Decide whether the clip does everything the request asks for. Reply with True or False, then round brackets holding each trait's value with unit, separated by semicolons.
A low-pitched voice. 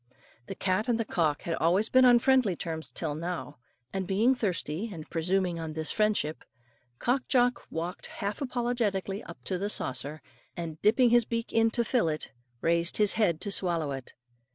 False (190 Hz)